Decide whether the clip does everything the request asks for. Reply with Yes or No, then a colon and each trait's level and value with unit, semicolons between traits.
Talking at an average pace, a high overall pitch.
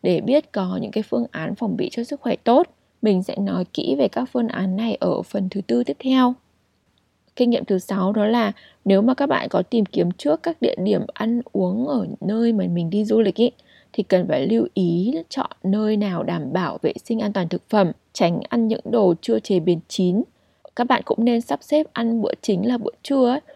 Yes: average, 230 wpm; high, 215 Hz